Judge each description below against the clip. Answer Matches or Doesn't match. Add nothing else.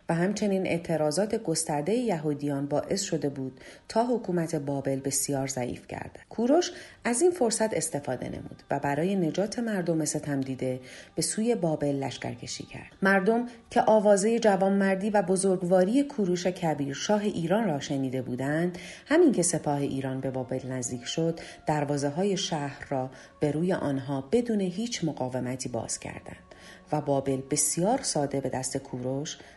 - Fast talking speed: Doesn't match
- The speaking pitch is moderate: Matches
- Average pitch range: Doesn't match